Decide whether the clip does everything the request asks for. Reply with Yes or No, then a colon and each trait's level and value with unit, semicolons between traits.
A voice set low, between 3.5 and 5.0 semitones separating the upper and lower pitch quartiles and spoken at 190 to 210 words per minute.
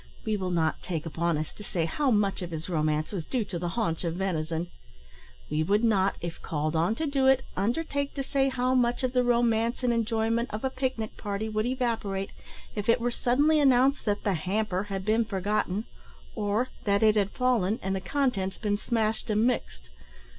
No: high, 215 Hz; average, 4.7 semitones; fast, 205 wpm